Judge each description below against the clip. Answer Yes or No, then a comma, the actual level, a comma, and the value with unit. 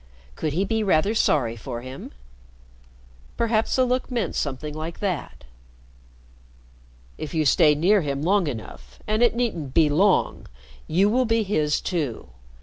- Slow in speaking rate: No, average, 145 wpm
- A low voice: No, medium, 165 Hz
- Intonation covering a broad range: Yes, wide, 6.6 semitones